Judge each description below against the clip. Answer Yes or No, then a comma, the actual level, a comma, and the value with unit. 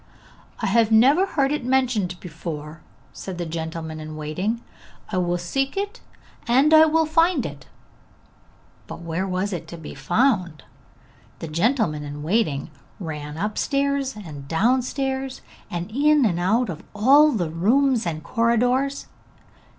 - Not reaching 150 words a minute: Yes, average, 140 wpm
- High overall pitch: Yes, high, 210 Hz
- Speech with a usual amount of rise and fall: No, wide, 8.4 semitones